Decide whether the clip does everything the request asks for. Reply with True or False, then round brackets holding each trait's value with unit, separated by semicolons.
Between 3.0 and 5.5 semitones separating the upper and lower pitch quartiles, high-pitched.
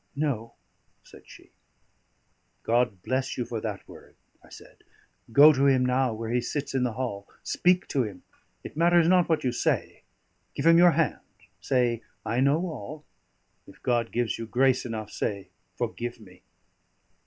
False (4.2 semitones; 125 Hz)